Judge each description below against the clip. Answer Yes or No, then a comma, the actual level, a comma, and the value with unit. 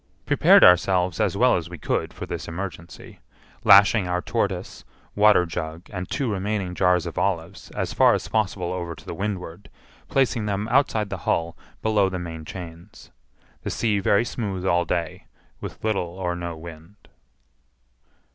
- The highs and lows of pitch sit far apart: No, average, 3.0 semitones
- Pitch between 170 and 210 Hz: No, very low, 90 Hz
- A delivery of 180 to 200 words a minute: No, average, 155 wpm